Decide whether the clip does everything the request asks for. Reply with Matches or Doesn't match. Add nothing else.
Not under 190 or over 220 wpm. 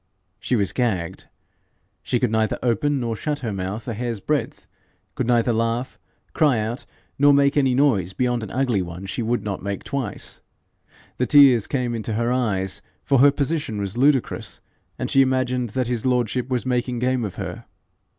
Doesn't match